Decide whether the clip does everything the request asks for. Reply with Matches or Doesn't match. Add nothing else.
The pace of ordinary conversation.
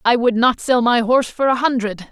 Doesn't match